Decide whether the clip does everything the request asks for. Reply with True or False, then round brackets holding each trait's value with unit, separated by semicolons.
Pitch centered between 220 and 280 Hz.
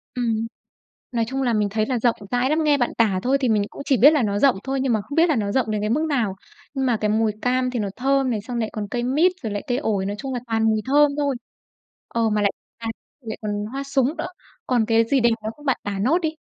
True (245 Hz)